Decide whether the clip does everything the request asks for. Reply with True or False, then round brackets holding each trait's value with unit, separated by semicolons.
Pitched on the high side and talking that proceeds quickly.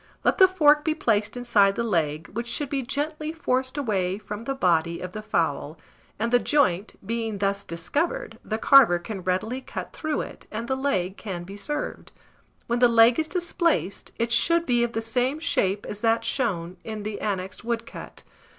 False (230 Hz; 185 wpm)